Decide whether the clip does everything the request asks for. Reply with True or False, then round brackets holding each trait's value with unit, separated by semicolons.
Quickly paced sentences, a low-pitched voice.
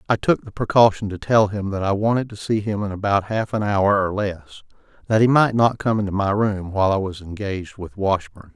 True (240 wpm; 100 Hz)